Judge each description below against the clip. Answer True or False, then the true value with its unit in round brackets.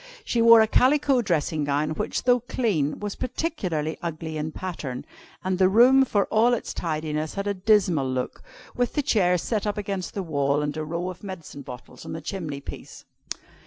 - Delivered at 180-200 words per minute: True (190 wpm)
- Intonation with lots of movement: True (6.1 semitones)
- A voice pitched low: False (185 Hz)